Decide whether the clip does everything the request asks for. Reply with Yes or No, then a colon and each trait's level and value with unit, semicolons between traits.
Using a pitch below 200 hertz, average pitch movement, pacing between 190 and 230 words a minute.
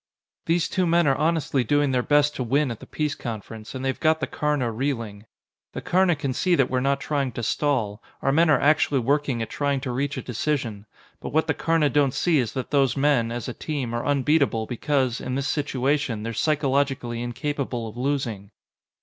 Yes: low, 135 Hz; average, 3.5 semitones; fast, 205 wpm